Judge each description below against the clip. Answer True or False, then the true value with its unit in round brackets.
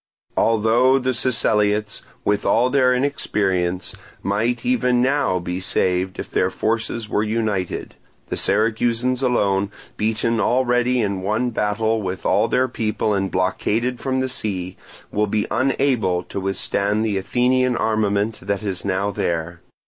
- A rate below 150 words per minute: True (140 wpm)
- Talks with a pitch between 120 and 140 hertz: False (110 Hz)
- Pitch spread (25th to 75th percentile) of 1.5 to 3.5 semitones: False (3.9 semitones)